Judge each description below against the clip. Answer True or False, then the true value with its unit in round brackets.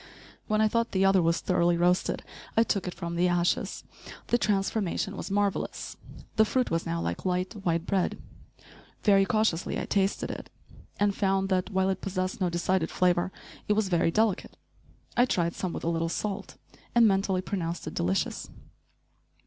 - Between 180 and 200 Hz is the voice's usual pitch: True (190 Hz)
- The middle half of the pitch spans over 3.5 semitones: False (2.8 semitones)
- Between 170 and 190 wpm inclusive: True (175 wpm)